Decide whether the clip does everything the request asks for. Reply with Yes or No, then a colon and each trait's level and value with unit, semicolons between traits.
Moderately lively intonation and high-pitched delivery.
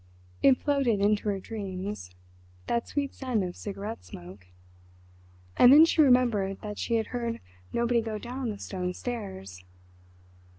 Yes: average, 5.0 semitones; high, 210 Hz